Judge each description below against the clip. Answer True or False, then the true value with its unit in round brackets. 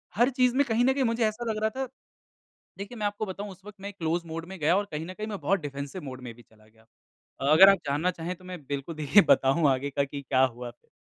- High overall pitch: False (175 Hz)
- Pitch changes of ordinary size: False (6.8 semitones)